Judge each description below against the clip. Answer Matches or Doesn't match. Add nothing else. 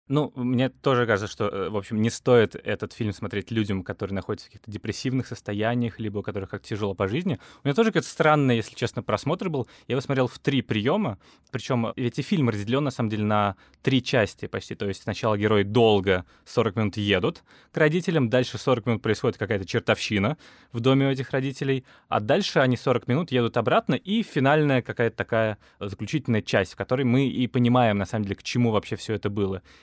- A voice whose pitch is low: Matches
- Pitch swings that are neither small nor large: Matches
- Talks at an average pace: Doesn't match